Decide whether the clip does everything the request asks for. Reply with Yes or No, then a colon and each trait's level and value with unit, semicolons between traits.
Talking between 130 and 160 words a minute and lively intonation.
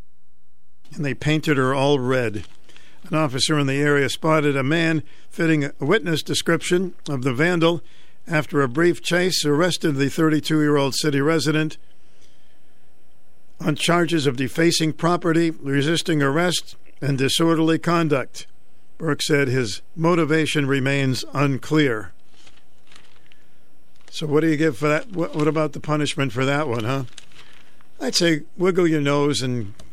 No: average, 140 wpm; average, 3.0 semitones